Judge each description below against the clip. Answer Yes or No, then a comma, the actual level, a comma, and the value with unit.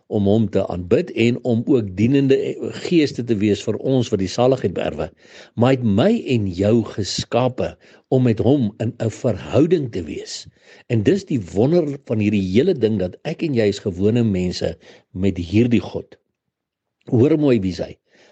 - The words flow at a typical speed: Yes, average, 180 wpm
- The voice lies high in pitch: No, low, 115 Hz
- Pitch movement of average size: Yes, average, 4.3 semitones